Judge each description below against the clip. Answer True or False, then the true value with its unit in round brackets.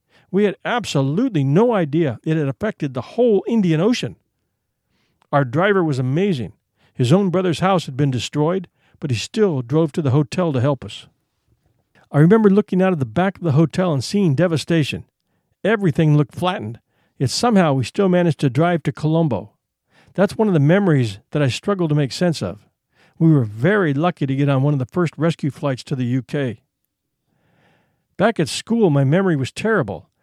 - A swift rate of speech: False (185 wpm)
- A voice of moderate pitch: True (155 Hz)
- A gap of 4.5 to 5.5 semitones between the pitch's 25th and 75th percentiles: True (5.2 semitones)